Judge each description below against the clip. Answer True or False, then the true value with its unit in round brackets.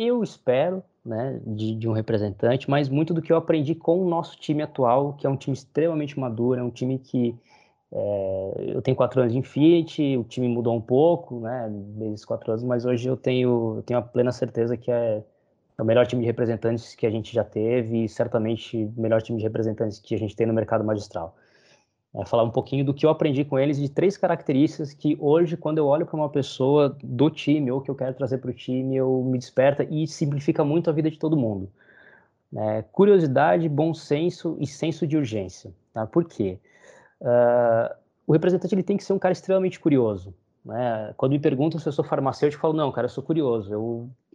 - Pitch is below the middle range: True (130 Hz)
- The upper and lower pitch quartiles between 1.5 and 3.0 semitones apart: False (5.1 semitones)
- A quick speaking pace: True (215 wpm)